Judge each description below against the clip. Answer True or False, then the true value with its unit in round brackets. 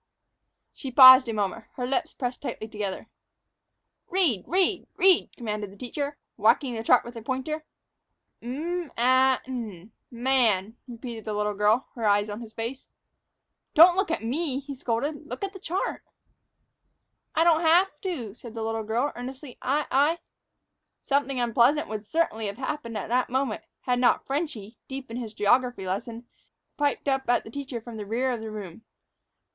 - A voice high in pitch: True (250 Hz)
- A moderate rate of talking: True (175 wpm)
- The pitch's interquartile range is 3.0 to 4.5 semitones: True (4.2 semitones)